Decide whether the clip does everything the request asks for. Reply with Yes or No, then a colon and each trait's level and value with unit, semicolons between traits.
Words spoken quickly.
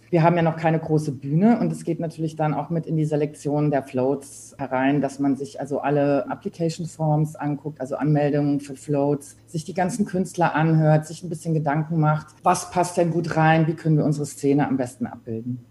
Yes: fast, 210 wpm